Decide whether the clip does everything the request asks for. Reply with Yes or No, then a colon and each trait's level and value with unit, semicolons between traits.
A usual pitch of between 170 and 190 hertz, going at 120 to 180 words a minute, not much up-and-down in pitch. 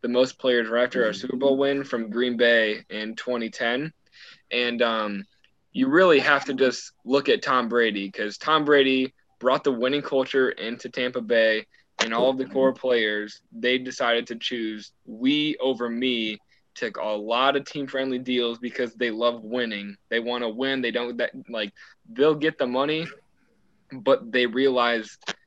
No: low, 125 Hz; average, 175 wpm; narrow, 2.2 semitones